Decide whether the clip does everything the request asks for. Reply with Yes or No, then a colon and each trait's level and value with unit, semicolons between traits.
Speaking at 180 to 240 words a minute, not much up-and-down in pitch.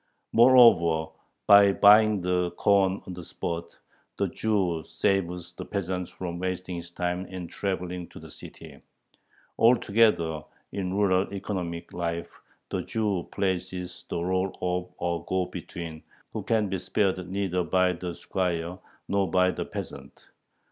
No: average, 140 wpm; narrow, 2.1 semitones